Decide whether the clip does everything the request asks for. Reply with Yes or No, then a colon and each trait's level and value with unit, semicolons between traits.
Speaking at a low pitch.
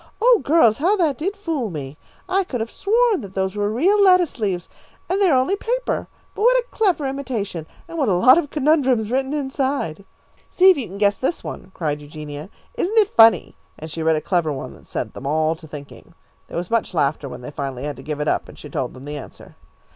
No: high, 225 Hz